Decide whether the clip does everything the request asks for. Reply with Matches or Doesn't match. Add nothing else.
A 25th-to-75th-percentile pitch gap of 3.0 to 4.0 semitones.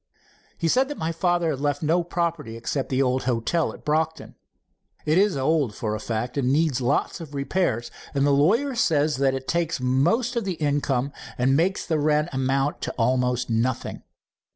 Doesn't match